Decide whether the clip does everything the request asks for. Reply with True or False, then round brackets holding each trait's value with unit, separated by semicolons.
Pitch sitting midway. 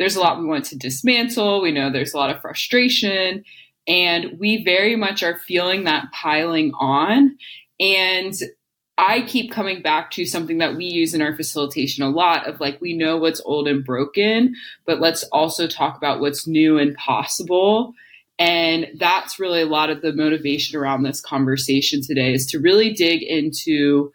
True (165 Hz)